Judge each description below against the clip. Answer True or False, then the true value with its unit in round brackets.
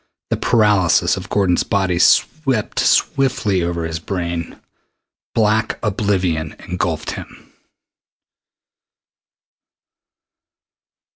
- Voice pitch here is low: True (95 Hz)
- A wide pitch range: False (3.6 semitones)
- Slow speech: True (75 wpm)